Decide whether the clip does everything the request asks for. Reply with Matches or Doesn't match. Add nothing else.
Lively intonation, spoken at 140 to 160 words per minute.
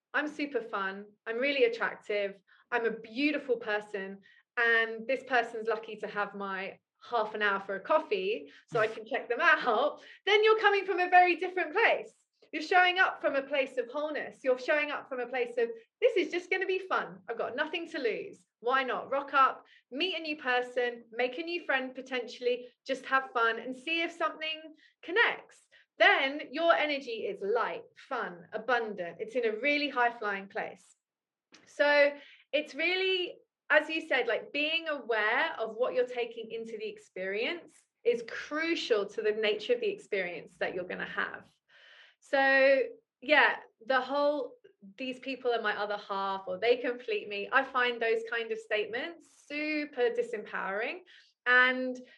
Doesn't match